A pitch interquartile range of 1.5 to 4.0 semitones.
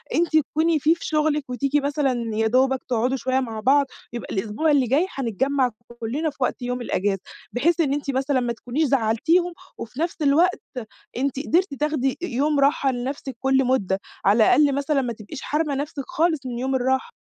Yes: average, 3.4 semitones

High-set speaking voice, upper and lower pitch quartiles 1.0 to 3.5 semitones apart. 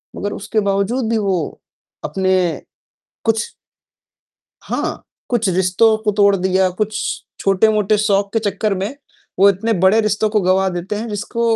Yes: high, 205 Hz; narrow, 2.4 semitones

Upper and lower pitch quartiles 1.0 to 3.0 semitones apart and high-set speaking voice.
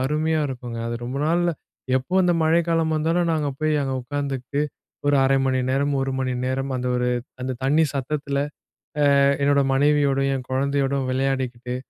No: narrow, 2.6 semitones; medium, 140 Hz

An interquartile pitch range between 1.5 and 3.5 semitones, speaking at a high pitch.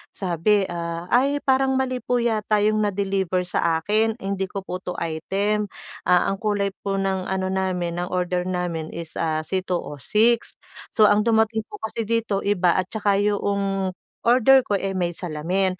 Yes: average, 3.0 semitones; high, 195 Hz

